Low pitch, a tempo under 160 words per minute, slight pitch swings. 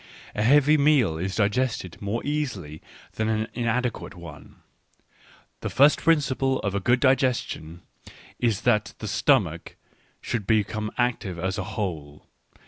No: low, 110 Hz; slow, 135 wpm; average, 5.3 semitones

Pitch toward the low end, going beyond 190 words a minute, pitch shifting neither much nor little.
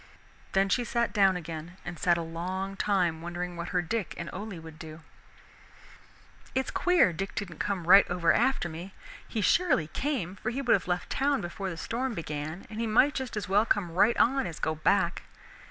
No: high, 190 Hz; average, 200 wpm; average, 4.8 semitones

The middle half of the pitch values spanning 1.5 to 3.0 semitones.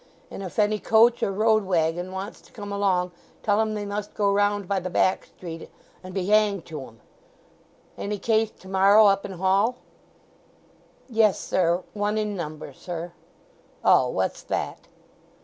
Yes: average, 2.7 semitones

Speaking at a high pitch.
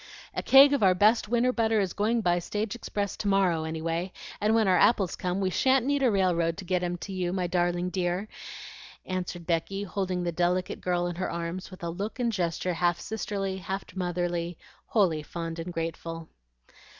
No: medium, 180 Hz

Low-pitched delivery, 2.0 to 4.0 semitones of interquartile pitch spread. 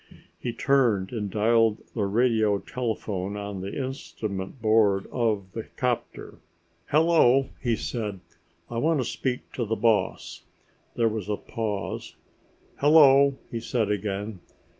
Yes: low, 110 Hz; average, 3.4 semitones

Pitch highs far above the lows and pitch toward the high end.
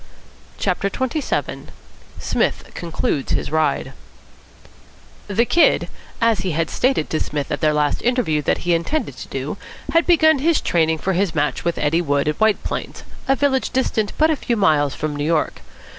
No: wide, 8.7 semitones; medium, 175 Hz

